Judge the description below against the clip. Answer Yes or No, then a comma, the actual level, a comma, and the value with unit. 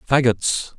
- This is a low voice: Yes, low, 120 Hz